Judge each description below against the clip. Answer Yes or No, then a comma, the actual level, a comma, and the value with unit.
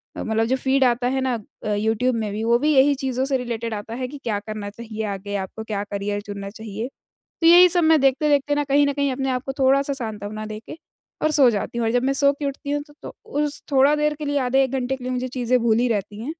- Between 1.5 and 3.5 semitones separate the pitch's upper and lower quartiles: No, average, 4.3 semitones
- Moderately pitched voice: No, very high, 250 Hz